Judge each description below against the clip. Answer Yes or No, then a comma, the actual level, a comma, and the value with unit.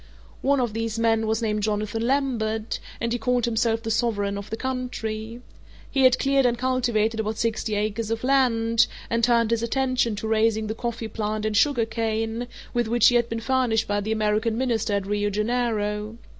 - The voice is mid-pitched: No, high, 225 Hz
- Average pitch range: No, narrow, 1.8 semitones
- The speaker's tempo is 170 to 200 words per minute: Yes, average, 190 wpm